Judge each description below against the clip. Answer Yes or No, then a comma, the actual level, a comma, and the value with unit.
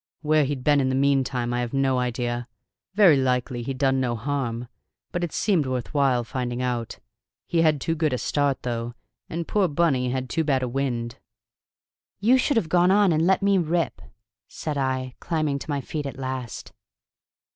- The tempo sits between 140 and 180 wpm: No, average, 190 wpm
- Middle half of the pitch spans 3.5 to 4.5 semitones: Yes, average, 3.9 semitones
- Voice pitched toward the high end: No, low, 135 Hz